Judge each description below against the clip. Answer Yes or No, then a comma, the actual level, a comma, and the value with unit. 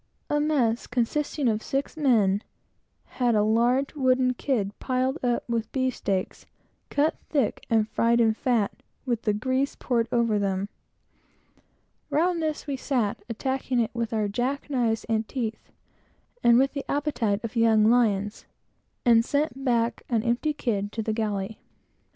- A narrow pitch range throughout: No, average, 3.4 semitones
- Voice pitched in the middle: No, high, 235 Hz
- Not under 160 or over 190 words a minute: No, average, 150 wpm